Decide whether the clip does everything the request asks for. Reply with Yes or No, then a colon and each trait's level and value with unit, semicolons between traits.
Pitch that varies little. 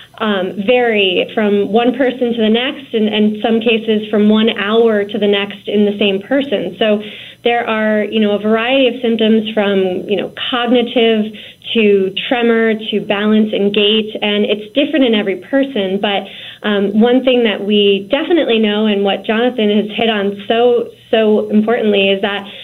Yes: narrow, 2.3 semitones